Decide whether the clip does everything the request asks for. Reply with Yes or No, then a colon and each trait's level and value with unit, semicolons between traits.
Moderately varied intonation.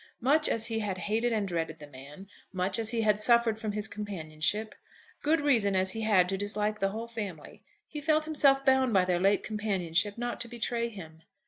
Yes: average, 3.8 semitones